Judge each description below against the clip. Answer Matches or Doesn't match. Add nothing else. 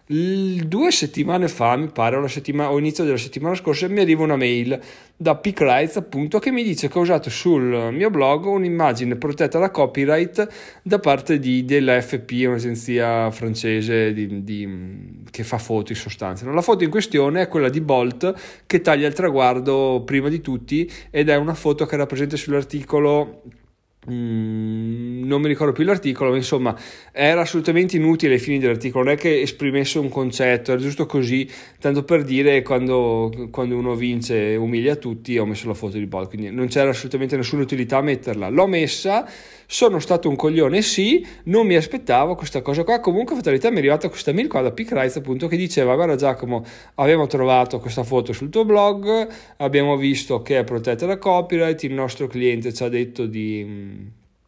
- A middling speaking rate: Doesn't match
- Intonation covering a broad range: Doesn't match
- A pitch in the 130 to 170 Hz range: Matches